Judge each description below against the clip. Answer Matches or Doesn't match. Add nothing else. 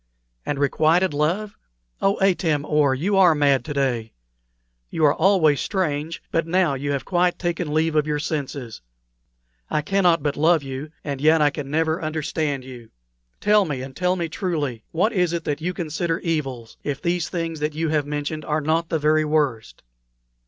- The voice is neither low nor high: Matches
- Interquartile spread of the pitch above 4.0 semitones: Doesn't match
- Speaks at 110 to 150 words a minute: Doesn't match